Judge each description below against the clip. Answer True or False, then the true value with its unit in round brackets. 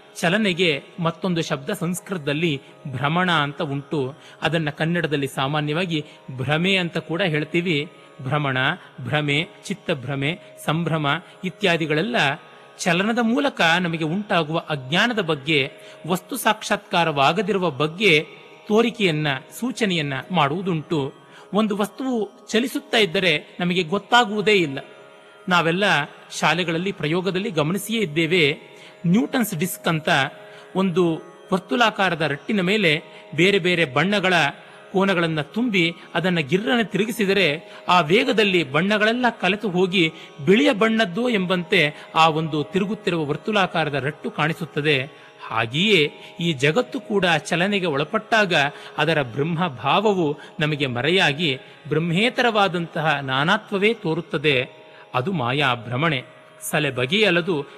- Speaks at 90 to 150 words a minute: True (95 wpm)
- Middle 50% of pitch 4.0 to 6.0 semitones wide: True (4.9 semitones)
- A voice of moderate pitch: True (170 Hz)